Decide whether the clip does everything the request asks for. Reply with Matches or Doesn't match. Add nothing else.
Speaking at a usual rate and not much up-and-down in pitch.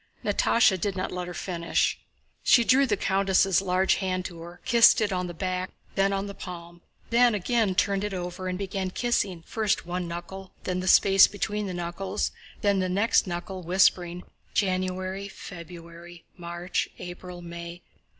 Matches